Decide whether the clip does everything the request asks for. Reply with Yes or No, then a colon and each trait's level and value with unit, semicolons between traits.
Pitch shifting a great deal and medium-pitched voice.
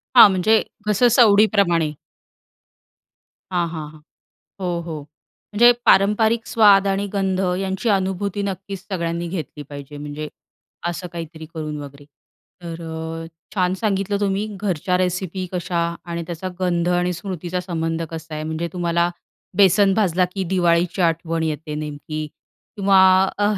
No: average, 3.1 semitones; medium, 180 Hz